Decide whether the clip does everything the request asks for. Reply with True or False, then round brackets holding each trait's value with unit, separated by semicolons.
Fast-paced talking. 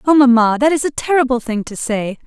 True (240 wpm)